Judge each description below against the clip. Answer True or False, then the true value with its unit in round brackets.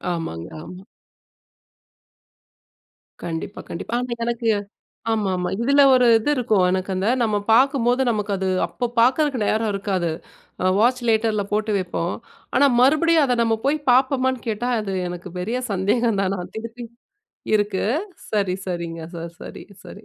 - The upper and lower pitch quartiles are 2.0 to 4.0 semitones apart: False (4.8 semitones)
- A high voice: True (220 Hz)